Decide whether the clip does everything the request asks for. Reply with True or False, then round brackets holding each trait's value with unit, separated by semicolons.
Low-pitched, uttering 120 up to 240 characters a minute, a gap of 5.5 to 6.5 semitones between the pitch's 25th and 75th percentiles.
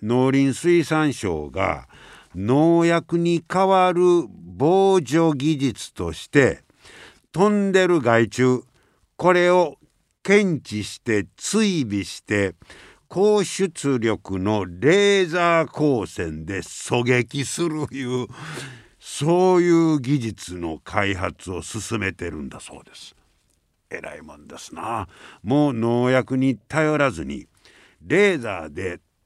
False (130 Hz; 200 characters per minute; 8.8 semitones)